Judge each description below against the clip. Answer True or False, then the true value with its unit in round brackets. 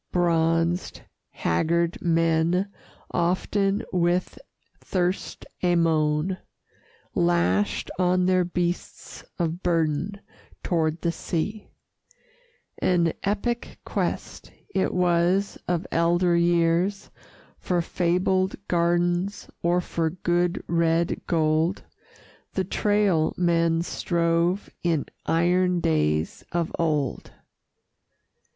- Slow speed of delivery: True (90 wpm)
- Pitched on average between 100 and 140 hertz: False (170 Hz)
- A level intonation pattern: True (1.6 semitones)